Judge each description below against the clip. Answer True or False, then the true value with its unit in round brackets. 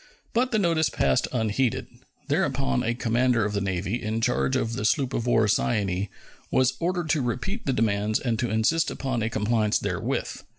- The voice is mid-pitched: False (115 Hz)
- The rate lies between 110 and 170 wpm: False (180 wpm)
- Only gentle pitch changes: False (3.7 semitones)